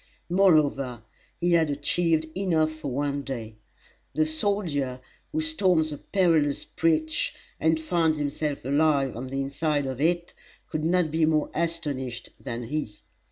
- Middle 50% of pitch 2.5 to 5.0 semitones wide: Yes, average, 3.0 semitones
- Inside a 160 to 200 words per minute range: No, average, 140 wpm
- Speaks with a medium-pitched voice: Yes, medium, 155 Hz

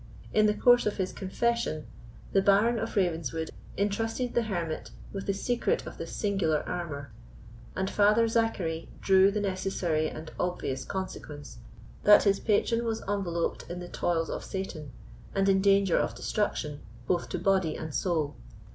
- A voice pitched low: No, high, 190 Hz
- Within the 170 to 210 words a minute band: No, average, 155 wpm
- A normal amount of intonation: Yes, average, 4.0 semitones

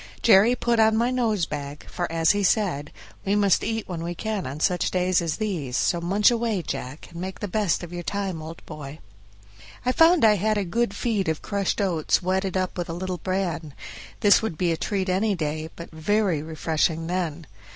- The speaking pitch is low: No, medium, 185 Hz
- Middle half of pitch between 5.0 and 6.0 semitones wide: No, average, 4.2 semitones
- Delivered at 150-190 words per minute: No, fast, 205 wpm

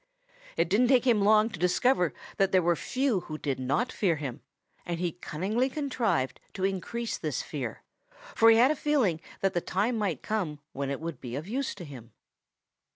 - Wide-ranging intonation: Yes, wide, 6.5 semitones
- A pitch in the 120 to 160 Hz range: No, high, 190 Hz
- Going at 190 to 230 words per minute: Yes, average, 195 wpm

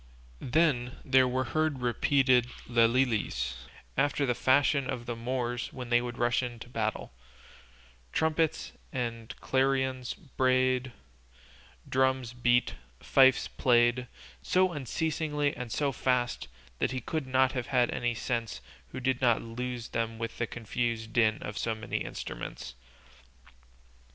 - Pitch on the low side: Yes, low, 125 Hz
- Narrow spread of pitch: Yes, narrow, 2.0 semitones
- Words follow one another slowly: Yes, slow, 125 wpm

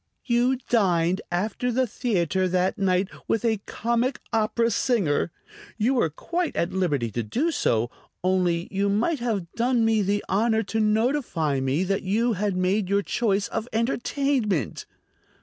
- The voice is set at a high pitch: Yes, high, 210 Hz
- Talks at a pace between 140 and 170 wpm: Yes, average, 150 wpm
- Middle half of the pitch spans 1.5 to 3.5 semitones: No, average, 4.5 semitones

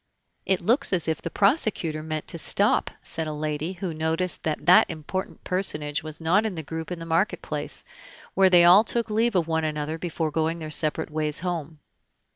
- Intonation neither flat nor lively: Yes, average, 3.0 semitones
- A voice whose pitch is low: No, medium, 165 Hz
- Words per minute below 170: No, average, 200 wpm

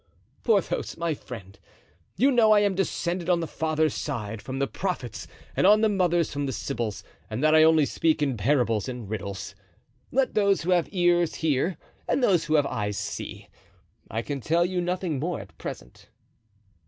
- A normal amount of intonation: No, wide, 6.5 semitones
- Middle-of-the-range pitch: Yes, medium, 160 Hz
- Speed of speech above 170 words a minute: Yes, average, 180 wpm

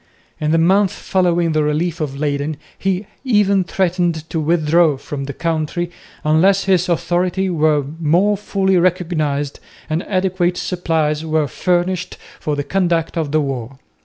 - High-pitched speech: No, medium, 170 Hz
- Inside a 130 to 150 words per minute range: Yes, average, 145 wpm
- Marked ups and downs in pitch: No, average, 3.2 semitones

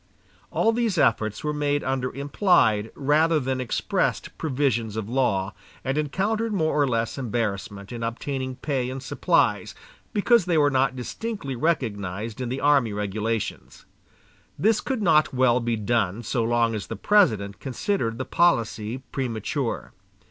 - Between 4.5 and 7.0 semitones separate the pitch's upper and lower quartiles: Yes, average, 4.9 semitones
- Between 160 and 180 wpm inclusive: No, average, 145 wpm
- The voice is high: No, low, 130 Hz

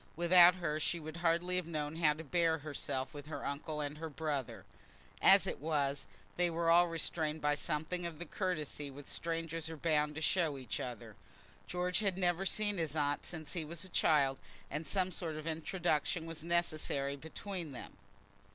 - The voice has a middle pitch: Yes, medium, 160 Hz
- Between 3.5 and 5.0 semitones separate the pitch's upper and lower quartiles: No, narrow, 2.6 semitones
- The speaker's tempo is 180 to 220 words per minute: Yes, average, 190 wpm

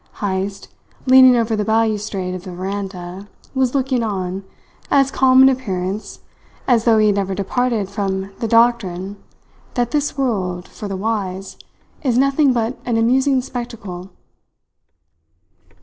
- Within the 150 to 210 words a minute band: No, slow, 135 wpm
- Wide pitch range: No, average, 4.5 semitones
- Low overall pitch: No, high, 215 Hz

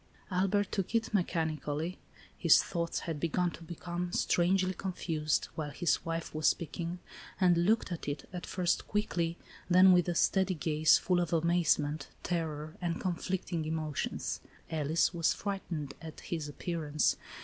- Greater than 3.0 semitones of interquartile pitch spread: No, narrow, 2.5 semitones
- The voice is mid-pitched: Yes, medium, 170 Hz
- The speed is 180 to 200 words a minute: No, average, 150 wpm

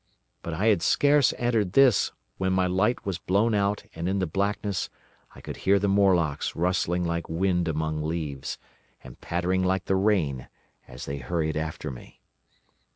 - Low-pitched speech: Yes, very low, 90 Hz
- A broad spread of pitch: No, average, 3.7 semitones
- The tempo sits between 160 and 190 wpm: Yes, average, 165 wpm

